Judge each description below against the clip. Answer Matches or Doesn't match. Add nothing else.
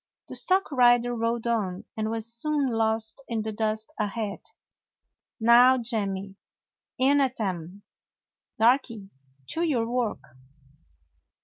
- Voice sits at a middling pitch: Doesn't match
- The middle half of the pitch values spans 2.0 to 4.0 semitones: Matches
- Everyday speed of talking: Doesn't match